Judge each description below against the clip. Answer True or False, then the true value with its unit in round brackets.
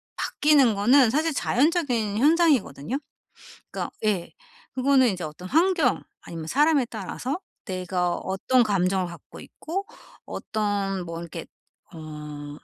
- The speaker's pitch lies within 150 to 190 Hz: False (215 Hz)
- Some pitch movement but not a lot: False (7.8 semitones)